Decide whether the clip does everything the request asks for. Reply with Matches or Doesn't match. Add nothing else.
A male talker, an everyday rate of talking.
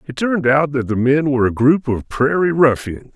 Doesn't match